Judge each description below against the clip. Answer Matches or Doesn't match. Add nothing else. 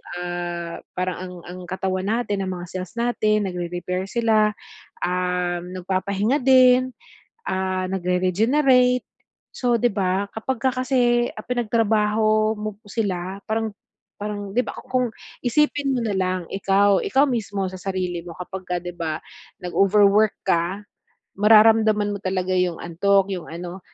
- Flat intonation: Doesn't match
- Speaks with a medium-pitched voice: Doesn't match